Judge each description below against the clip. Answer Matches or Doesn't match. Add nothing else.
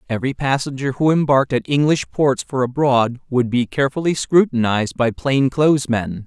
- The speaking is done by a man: Matches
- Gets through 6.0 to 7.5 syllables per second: Doesn't match